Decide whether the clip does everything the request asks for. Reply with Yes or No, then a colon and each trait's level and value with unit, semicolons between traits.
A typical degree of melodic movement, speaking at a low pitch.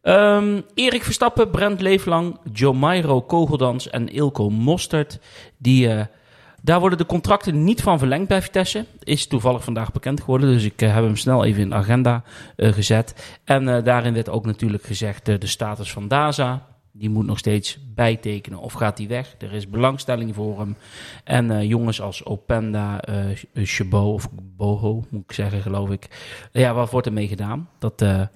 Yes: average, 4.8 semitones; low, 120 Hz